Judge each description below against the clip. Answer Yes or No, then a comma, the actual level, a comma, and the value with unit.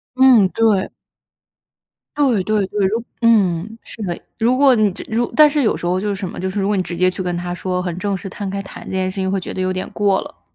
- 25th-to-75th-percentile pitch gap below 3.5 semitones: Yes, average, 3.1 semitones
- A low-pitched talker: No, high, 195 Hz